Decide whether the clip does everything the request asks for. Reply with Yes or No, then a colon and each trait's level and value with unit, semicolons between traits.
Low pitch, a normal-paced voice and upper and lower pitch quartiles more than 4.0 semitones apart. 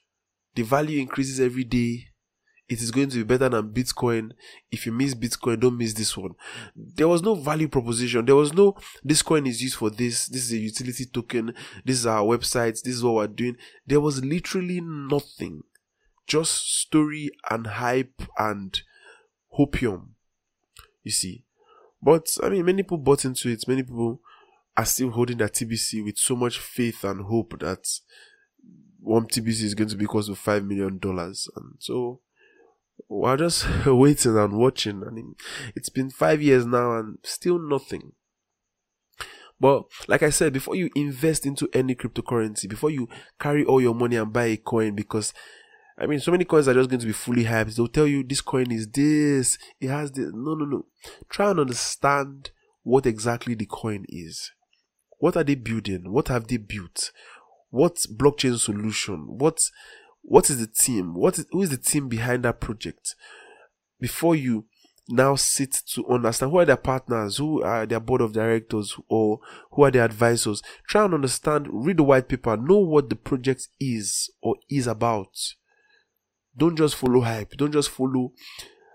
Yes: low, 130 Hz; average, 180 wpm; average, 4.5 semitones